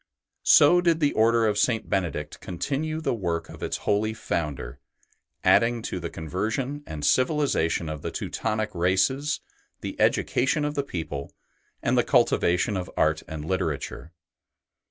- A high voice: No, low, 105 Hz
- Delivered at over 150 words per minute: No, average, 145 wpm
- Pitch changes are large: Yes, wide, 8.3 semitones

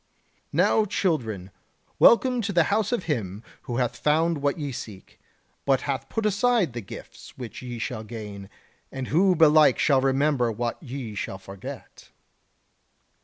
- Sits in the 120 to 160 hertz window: Yes, low, 135 Hz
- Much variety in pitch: Yes, wide, 6.7 semitones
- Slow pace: No, average, 150 wpm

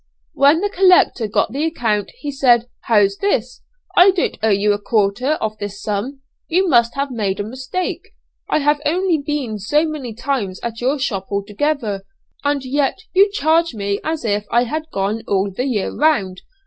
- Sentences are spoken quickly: No, average, 180 wpm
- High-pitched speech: Yes, very high, 250 Hz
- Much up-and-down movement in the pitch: Yes, wide, 6.4 semitones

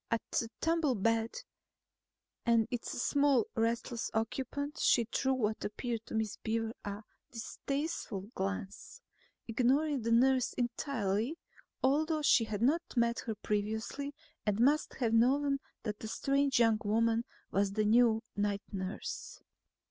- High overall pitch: Yes, high, 230 Hz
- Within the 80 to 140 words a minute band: Yes, slow, 135 wpm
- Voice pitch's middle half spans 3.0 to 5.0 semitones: Yes, average, 3.5 semitones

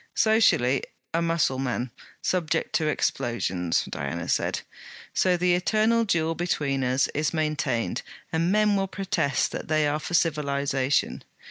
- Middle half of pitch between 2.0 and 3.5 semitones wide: No, average, 4.8 semitones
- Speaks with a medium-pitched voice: Yes, medium, 155 Hz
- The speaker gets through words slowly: Yes, slow, 130 wpm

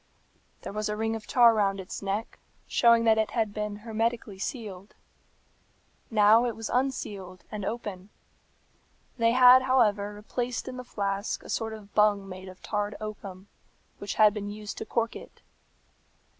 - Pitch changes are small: Yes, narrow, 2.2 semitones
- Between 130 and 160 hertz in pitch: No, high, 215 Hz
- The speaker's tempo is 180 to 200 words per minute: No, average, 160 wpm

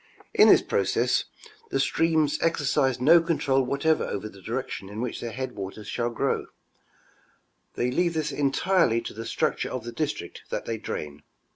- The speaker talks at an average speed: Yes, average, 160 wpm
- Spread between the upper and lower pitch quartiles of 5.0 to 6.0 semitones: Yes, wide, 5.6 semitones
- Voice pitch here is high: No, low, 130 Hz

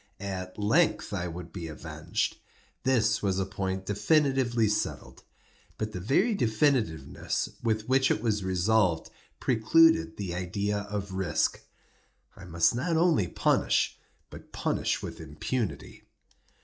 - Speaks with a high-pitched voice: No, low, 105 Hz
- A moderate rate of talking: No, slow, 125 wpm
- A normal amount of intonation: Yes, average, 4.7 semitones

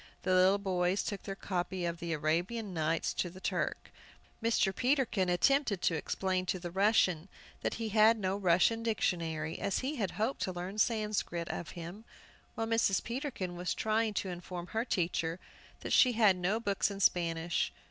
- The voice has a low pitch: No, high, 190 Hz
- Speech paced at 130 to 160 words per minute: No, average, 175 wpm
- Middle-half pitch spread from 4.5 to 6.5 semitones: No, average, 3.7 semitones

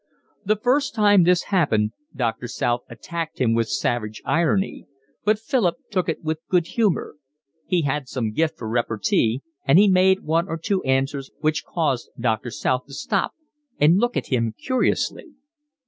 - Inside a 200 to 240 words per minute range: No, average, 165 wpm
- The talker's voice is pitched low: No, medium, 155 Hz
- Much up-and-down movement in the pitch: Yes, wide, 7.7 semitones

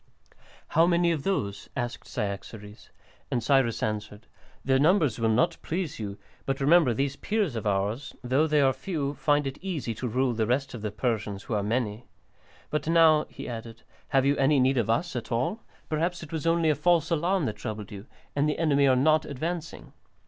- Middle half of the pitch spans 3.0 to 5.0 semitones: No, wide, 5.6 semitones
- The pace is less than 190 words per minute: No, average, 195 wpm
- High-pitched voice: No, low, 135 Hz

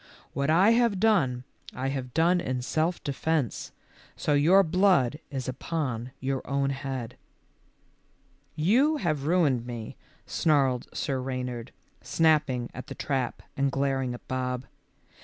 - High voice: No, medium, 140 Hz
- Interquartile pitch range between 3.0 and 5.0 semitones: Yes, average, 4.2 semitones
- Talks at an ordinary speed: No, slow, 130 wpm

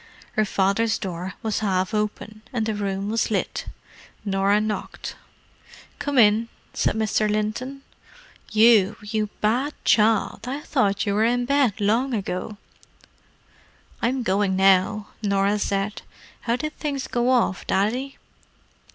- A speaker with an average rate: No, slow, 130 wpm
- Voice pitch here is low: No, high, 215 Hz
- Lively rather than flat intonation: No, average, 3.1 semitones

